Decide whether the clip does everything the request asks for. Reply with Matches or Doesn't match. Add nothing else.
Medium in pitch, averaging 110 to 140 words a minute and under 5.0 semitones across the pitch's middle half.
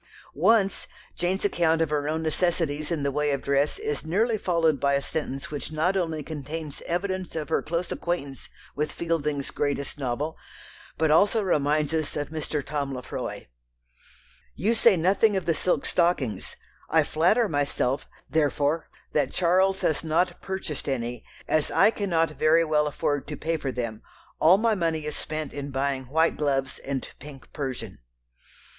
Doesn't match